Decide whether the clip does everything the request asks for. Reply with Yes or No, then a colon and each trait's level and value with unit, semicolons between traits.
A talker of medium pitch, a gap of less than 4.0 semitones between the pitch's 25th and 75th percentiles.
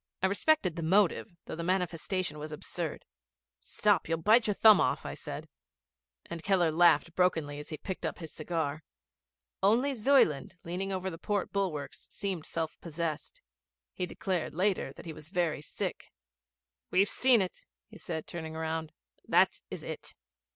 Yes: medium, 175 Hz; average, 3.4 semitones